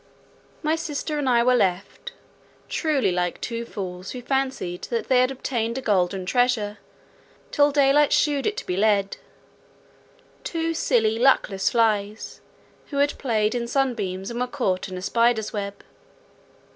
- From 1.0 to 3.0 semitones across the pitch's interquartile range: No, average, 5.2 semitones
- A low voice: No, high, 235 Hz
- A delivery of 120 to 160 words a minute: Yes, average, 145 wpm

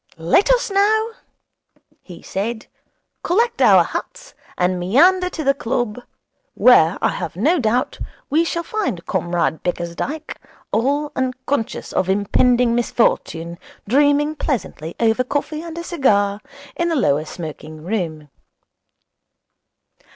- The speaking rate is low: Yes, slow, 120 wpm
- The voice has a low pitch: No, high, 245 Hz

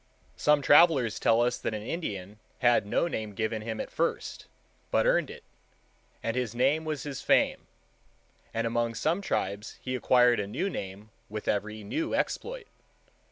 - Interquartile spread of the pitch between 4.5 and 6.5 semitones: Yes, average, 5.2 semitones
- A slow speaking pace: No, average, 160 wpm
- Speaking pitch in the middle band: No, low, 115 Hz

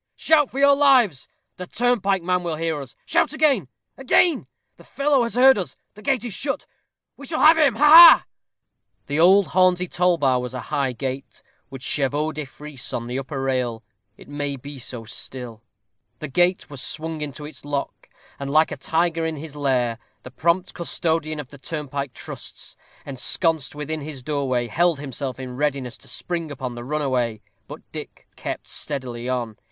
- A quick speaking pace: No, average, 180 wpm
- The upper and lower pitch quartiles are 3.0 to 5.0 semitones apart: No, wide, 5.5 semitones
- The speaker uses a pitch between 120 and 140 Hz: No, medium, 150 Hz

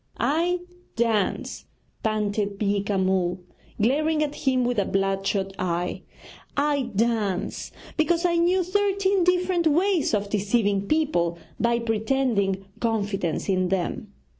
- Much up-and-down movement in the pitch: Yes, wide, 7.8 semitones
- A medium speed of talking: No, slow, 115 wpm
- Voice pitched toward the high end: Yes, high, 225 Hz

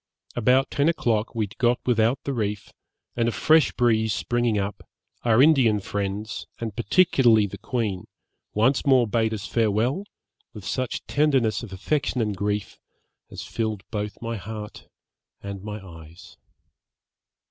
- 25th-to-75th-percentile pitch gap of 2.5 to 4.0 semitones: Yes, average, 3.0 semitones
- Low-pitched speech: Yes, low, 110 Hz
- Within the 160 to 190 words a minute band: No, average, 145 wpm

